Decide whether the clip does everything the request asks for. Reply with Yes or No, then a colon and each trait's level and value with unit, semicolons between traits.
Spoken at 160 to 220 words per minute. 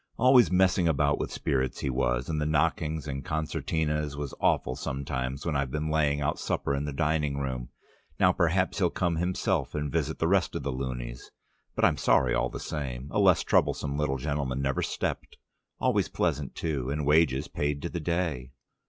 Yes: average, 190 wpm